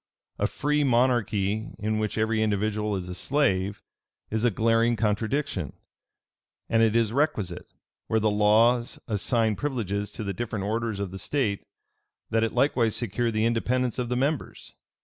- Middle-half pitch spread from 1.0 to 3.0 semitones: Yes, narrow, 2.6 semitones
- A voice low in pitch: Yes, low, 110 Hz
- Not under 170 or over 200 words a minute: No, average, 155 wpm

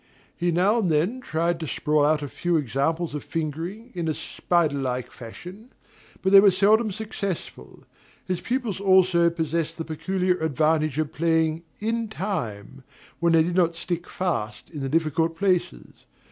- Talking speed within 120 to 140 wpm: No, average, 160 wpm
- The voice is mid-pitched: Yes, medium, 170 Hz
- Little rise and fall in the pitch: No, average, 3.4 semitones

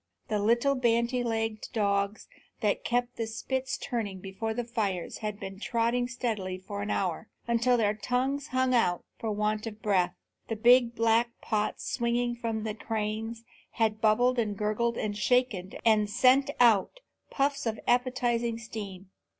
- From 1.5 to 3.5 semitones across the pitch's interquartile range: Yes, narrow, 2.6 semitones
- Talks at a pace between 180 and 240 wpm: No, average, 160 wpm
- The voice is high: Yes, high, 225 Hz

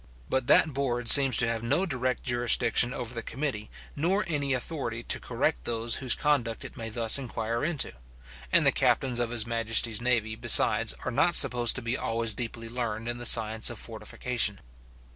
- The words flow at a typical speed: Yes, average, 180 wpm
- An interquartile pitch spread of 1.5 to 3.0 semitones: Yes, narrow, 2.4 semitones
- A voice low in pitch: Yes, low, 120 Hz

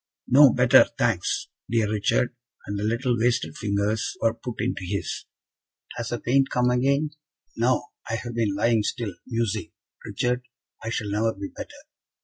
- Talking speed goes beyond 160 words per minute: No, average, 155 wpm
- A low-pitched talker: Yes, low, 115 Hz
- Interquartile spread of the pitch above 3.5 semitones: No, average, 2.8 semitones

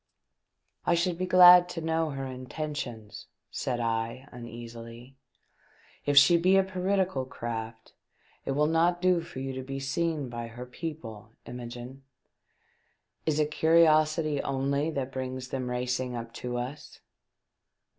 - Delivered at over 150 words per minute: No, average, 145 wpm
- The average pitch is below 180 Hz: Yes, low, 135 Hz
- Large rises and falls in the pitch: No, average, 4.9 semitones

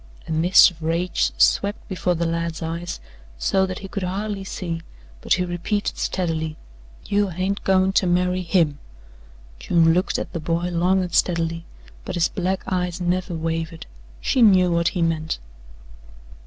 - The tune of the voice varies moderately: No, narrow, 2.1 semitones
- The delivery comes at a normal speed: Yes, average, 160 wpm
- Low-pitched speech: No, medium, 175 Hz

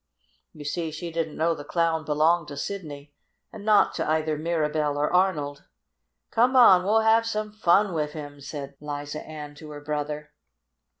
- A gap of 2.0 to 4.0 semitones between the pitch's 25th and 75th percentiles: Yes, average, 3.4 semitones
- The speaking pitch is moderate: Yes, medium, 155 Hz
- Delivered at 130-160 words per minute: No, average, 170 wpm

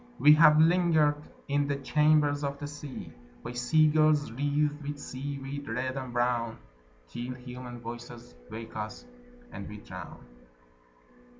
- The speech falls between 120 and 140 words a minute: Yes, slow, 135 wpm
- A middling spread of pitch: Yes, average, 3.3 semitones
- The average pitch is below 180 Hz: Yes, medium, 140 Hz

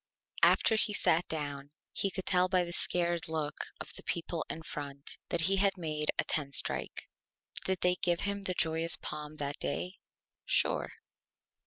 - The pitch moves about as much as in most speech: Yes, average, 3.3 semitones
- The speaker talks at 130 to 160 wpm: No, average, 170 wpm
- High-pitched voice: No, medium, 170 Hz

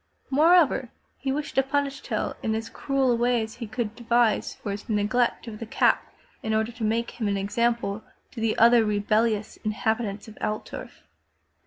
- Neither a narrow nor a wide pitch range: No, narrow, 2.3 semitones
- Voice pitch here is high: Yes, high, 225 Hz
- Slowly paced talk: No, average, 180 wpm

